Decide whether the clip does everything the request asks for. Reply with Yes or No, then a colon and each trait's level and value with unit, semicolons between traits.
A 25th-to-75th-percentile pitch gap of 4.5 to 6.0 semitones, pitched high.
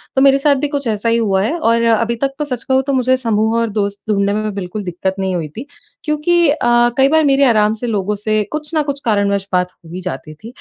Yes: average, 5.3 semitones; high, 230 Hz